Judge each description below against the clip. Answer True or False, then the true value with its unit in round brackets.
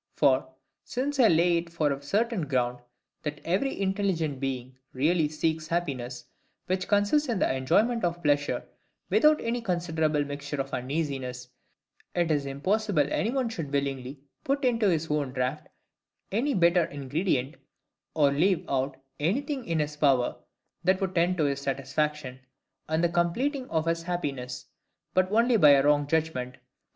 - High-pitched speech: False (160 Hz)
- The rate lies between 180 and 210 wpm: False (155 wpm)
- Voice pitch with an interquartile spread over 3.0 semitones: True (5.2 semitones)